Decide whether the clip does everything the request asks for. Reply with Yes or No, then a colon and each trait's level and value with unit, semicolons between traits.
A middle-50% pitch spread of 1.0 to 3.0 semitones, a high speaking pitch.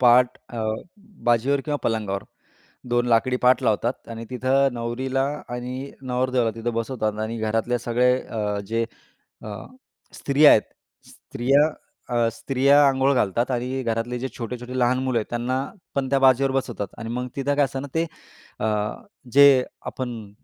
No: narrow, 2.5 semitones; low, 125 Hz